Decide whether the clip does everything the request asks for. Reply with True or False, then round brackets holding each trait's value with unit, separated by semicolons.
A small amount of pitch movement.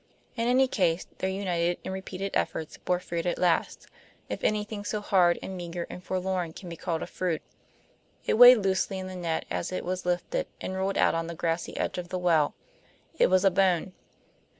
True (1.9 semitones)